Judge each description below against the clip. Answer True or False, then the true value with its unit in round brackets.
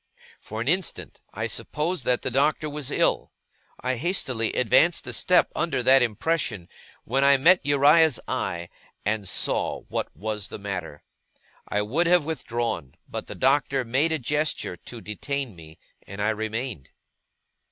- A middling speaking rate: True (150 wpm)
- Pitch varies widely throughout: True (6.0 semitones)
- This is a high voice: False (125 Hz)